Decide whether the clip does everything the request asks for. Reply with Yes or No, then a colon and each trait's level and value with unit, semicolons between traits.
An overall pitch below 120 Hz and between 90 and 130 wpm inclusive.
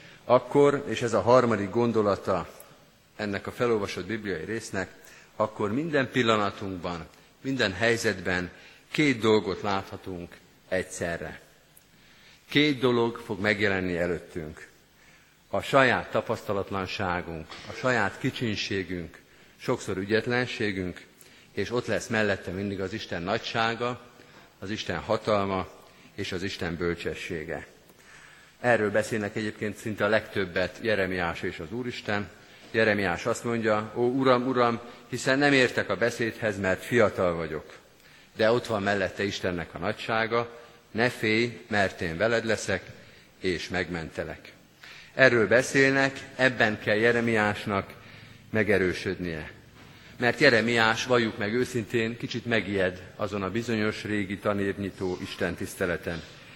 Yes: low, 105 Hz; average, 115 wpm